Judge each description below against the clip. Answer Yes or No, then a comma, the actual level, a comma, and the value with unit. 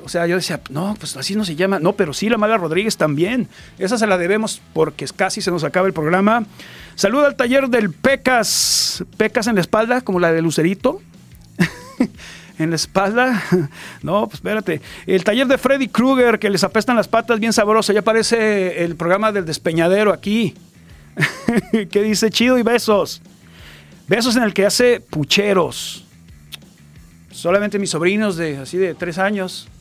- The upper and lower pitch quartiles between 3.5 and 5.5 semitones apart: Yes, average, 4.5 semitones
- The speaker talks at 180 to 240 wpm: No, average, 170 wpm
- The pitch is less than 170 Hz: No, high, 195 Hz